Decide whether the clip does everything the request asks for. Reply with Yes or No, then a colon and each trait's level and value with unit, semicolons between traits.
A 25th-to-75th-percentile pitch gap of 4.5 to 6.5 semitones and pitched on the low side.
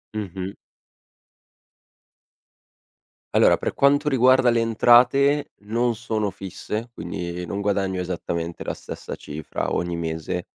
Yes: wide, 5.5 semitones; low, 100 Hz